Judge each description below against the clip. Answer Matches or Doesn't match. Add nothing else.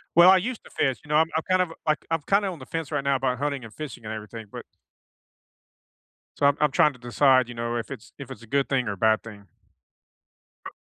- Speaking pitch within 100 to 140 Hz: Matches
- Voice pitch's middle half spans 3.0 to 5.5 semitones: Matches